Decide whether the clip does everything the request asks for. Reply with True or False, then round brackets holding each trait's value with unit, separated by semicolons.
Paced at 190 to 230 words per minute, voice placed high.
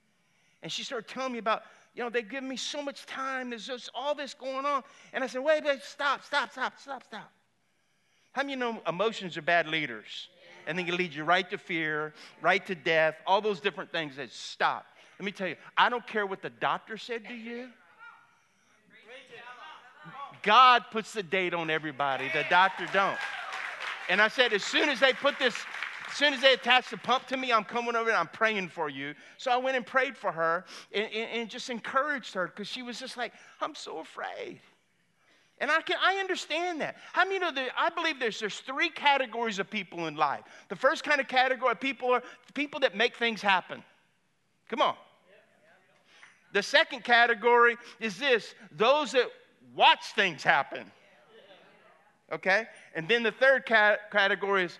True (195 wpm; 235 Hz)